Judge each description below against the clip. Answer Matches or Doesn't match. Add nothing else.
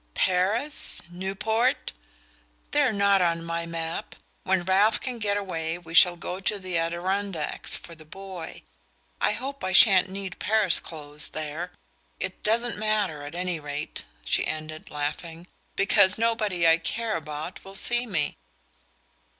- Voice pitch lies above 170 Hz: Matches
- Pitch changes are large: Doesn't match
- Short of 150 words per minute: Matches